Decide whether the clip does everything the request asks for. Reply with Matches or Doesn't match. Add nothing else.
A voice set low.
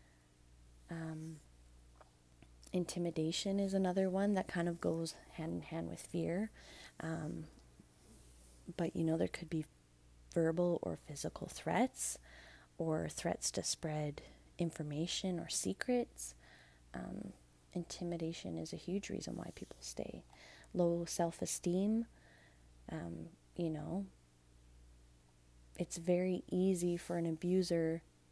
Doesn't match